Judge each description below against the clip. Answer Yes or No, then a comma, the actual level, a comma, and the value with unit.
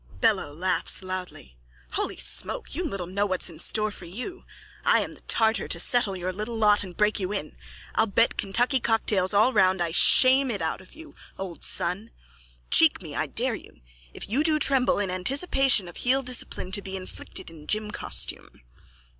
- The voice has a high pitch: Yes, high, 205 Hz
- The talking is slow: No, average, 185 wpm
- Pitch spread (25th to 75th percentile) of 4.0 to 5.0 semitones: Yes, average, 4.7 semitones